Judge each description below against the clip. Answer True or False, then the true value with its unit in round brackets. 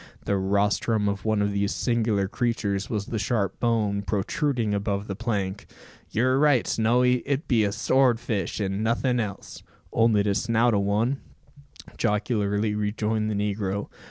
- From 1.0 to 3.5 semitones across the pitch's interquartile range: True (2.6 semitones)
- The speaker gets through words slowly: False (155 wpm)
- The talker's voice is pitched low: True (105 Hz)